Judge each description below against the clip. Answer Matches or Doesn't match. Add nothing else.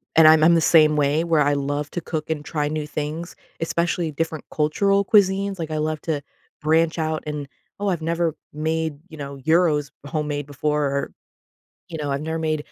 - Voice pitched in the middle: Matches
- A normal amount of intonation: Doesn't match